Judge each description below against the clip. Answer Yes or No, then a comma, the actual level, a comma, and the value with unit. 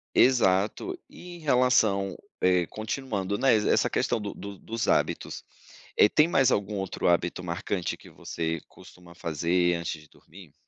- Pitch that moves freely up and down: No, average, 4.8 semitones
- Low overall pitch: Yes, low, 100 Hz